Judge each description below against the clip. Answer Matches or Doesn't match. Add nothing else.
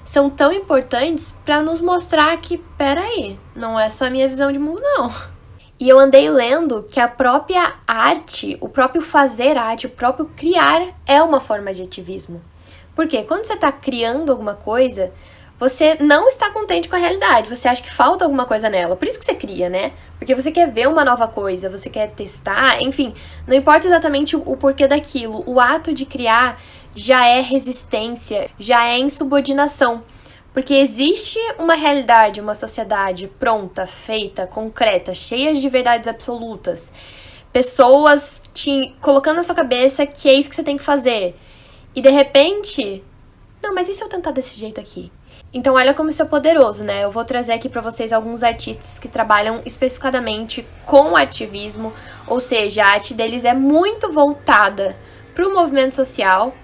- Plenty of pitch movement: Doesn't match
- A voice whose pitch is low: Doesn't match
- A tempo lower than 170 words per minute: Doesn't match